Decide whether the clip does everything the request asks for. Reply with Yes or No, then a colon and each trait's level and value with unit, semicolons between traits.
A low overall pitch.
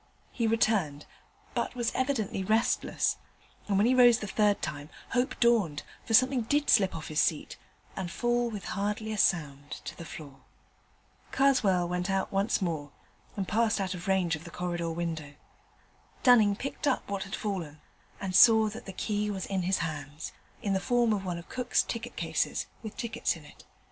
No: high, 195 Hz